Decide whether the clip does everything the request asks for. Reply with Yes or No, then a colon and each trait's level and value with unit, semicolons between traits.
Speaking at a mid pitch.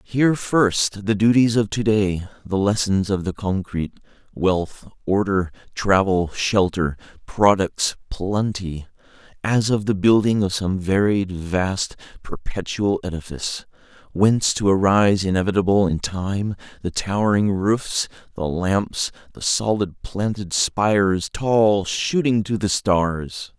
No: low, 100 Hz